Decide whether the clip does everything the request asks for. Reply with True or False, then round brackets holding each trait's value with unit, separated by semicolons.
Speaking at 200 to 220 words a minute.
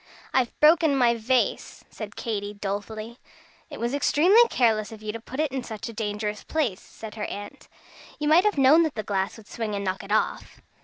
True (205 wpm)